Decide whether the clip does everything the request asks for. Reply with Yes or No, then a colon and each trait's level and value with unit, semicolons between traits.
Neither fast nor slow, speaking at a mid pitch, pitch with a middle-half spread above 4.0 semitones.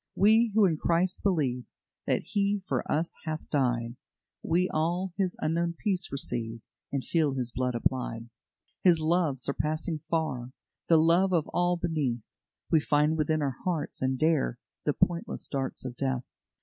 Yes: average, 155 wpm; medium, 155 Hz; average, 4.9 semitones